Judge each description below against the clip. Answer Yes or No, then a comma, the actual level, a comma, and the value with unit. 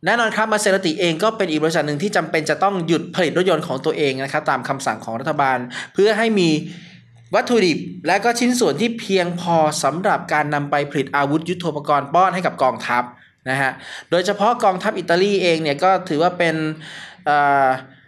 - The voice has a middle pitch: Yes, medium, 165 Hz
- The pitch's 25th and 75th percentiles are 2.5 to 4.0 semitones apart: No, average, 4.8 semitones